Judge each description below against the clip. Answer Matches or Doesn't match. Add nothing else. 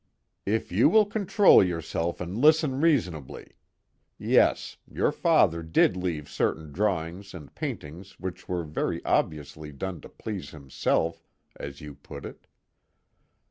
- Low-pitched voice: Matches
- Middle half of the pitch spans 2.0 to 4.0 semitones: Doesn't match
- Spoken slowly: Matches